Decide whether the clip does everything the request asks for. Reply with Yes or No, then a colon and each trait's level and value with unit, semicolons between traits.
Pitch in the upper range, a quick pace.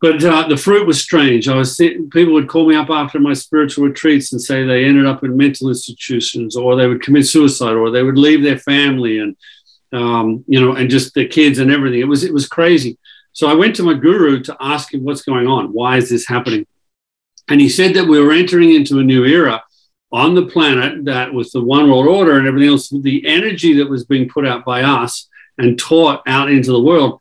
No: medium, 140 Hz; fast, 235 wpm